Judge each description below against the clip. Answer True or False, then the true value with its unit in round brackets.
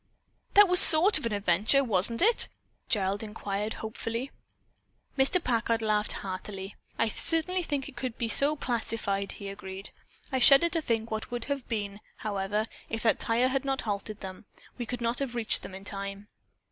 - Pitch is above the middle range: True (225 Hz)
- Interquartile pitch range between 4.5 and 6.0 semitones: True (4.8 semitones)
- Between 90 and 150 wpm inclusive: False (180 wpm)